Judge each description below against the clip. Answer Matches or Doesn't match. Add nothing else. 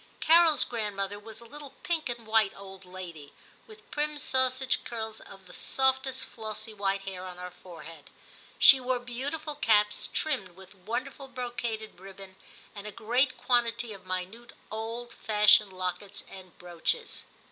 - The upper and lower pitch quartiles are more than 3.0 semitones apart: Matches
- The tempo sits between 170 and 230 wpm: Doesn't match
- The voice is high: Matches